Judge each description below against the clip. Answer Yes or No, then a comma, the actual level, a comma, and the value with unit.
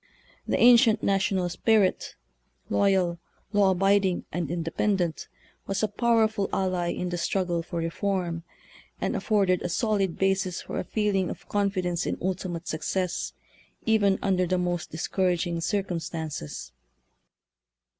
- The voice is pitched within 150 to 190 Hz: Yes, medium, 185 Hz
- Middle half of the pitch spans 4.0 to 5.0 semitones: No, narrow, 2.5 semitones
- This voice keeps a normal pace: No, slow, 130 wpm